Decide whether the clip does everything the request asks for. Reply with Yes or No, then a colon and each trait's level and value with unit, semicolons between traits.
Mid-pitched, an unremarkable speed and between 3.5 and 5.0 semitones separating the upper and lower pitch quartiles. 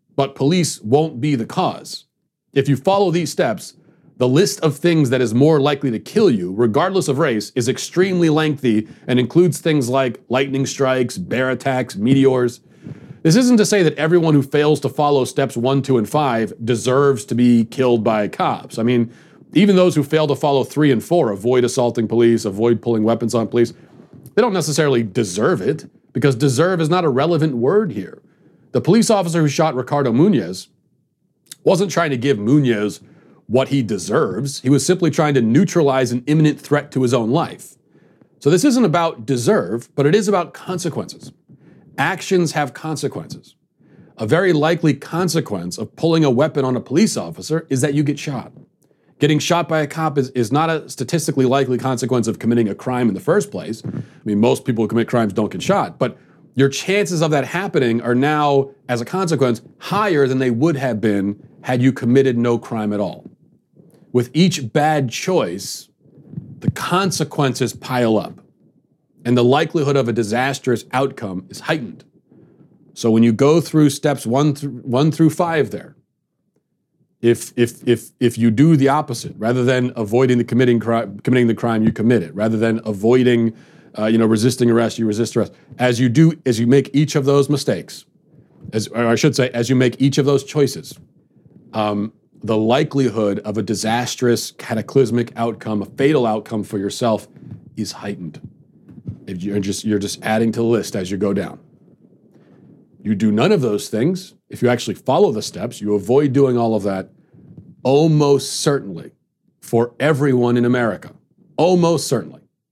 No: low, 130 Hz; average, 180 wpm; average, 4.5 semitones